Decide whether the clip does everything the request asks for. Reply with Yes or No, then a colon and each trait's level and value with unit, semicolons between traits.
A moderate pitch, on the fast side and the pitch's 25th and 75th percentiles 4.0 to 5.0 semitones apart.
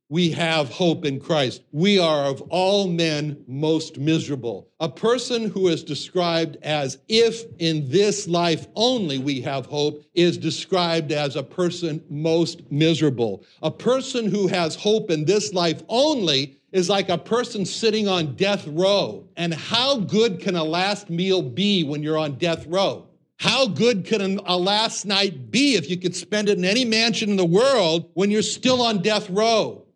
No: medium, 175 Hz; average, 175 wpm; average, 4.4 semitones